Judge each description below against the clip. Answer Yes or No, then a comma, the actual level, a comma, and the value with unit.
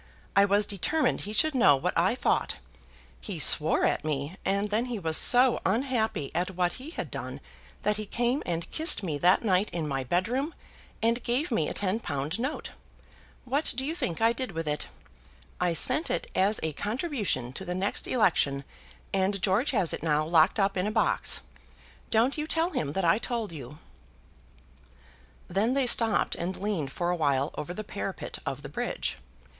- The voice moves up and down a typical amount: No, wide, 6.3 semitones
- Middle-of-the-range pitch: No, high, 200 Hz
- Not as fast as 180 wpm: No, average, 185 wpm